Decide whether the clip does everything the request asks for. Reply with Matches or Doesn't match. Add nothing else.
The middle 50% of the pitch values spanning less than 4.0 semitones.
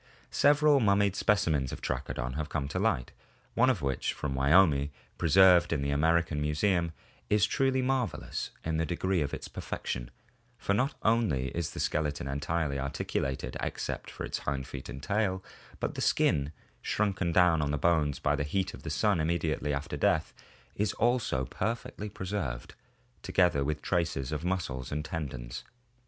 Doesn't match